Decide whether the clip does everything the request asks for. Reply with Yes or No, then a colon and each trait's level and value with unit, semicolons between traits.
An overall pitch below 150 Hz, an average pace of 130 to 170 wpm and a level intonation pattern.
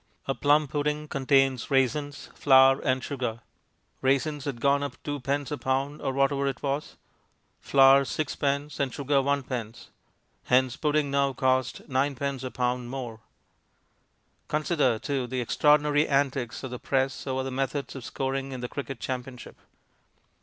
Yes: low, 135 Hz; average, 150 wpm; narrow, 1.7 semitones